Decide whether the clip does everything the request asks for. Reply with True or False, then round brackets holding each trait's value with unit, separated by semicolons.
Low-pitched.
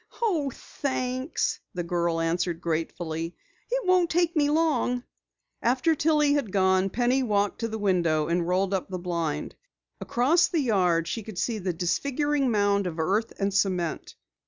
False (205 Hz)